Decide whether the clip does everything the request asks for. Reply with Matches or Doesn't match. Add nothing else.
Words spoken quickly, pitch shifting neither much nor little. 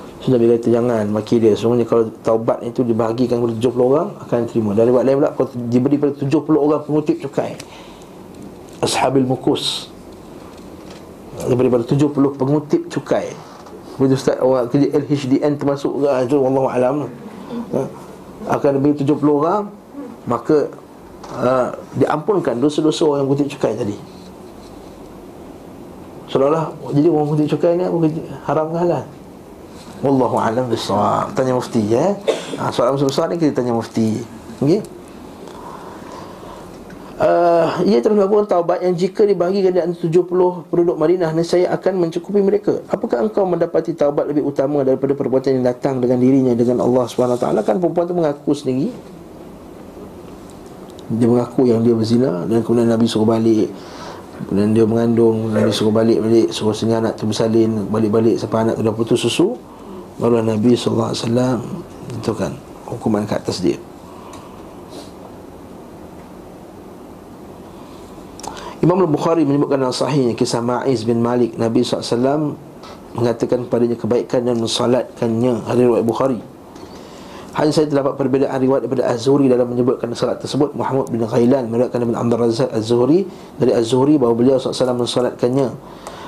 Doesn't match